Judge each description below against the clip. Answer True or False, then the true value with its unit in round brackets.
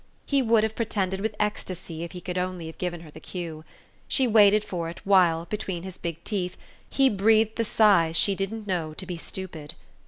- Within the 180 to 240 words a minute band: True (205 wpm)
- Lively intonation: False (3.8 semitones)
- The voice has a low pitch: False (185 Hz)